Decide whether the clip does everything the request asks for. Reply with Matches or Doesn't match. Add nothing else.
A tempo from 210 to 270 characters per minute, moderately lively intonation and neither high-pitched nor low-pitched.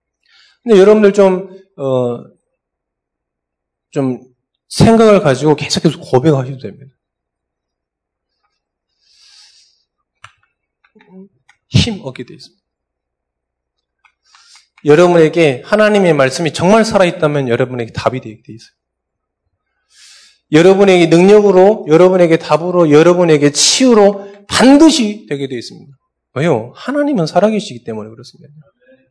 Doesn't match